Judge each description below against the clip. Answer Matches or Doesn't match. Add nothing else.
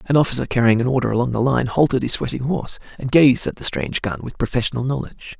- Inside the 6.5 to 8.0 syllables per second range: Matches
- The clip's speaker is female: Doesn't match